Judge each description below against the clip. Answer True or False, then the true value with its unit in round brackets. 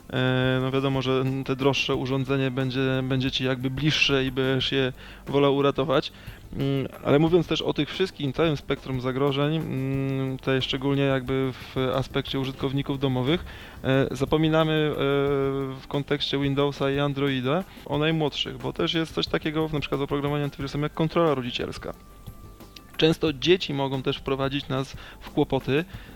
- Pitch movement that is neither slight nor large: False (1.4 semitones)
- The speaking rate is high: False (140 wpm)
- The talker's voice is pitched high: False (135 Hz)